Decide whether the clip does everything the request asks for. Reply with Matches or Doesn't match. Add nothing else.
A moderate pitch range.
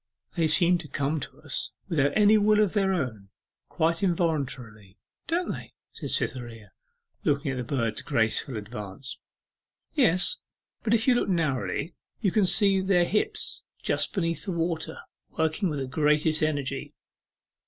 Doesn't match